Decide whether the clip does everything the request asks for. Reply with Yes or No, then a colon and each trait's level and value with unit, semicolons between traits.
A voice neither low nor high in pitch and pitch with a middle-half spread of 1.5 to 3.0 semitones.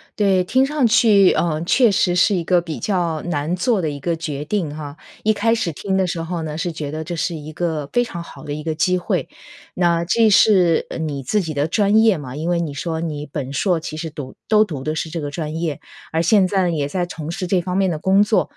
No: medium, 170 Hz; average, 3.7 semitones